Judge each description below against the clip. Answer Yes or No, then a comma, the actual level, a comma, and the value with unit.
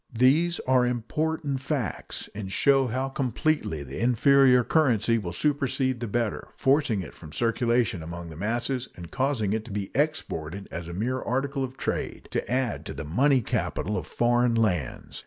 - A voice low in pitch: Yes, low, 120 Hz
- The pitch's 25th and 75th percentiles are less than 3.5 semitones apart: No, average, 4.8 semitones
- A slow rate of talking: No, average, 170 wpm